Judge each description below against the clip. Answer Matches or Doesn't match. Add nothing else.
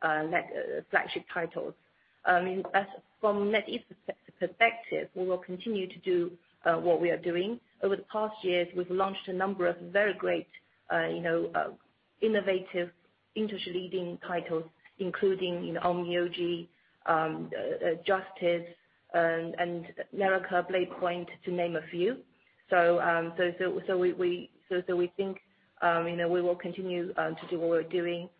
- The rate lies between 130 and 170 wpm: Matches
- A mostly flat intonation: Matches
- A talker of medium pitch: Matches